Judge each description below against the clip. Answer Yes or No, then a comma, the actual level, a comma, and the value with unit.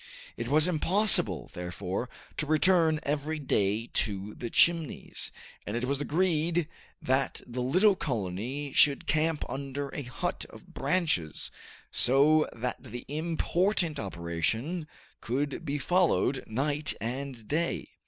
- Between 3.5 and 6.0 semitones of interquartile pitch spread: Yes, average, 4.8 semitones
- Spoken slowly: Yes, slow, 125 wpm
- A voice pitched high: No, medium, 140 Hz